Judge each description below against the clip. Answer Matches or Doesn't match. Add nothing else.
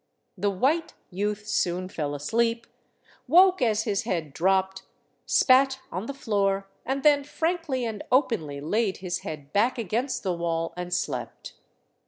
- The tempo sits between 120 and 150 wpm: Matches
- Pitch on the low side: Doesn't match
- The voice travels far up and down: Matches